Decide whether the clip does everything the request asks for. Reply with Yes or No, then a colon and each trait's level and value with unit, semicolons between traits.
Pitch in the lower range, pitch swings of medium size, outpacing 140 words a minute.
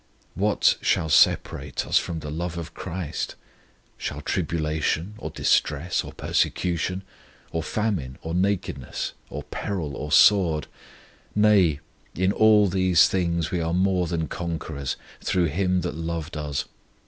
No: very low, 85 Hz; average, 3.1 semitones; slow, 135 wpm